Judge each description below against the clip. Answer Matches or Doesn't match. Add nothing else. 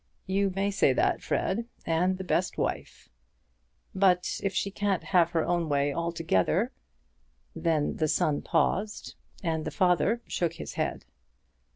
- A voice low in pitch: Doesn't match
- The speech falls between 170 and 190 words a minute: Doesn't match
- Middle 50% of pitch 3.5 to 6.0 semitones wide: Doesn't match